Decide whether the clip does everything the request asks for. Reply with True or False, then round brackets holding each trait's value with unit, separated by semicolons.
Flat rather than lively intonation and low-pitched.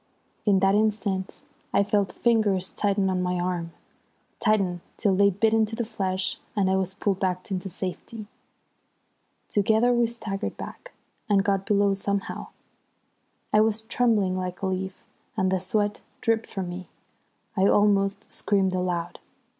False (2.1 semitones; 195 Hz)